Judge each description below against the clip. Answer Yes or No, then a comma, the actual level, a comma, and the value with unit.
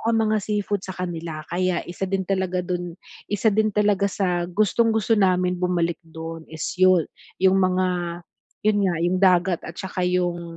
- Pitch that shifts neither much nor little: No, narrow, 2.3 semitones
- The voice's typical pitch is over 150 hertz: Yes, medium, 185 Hz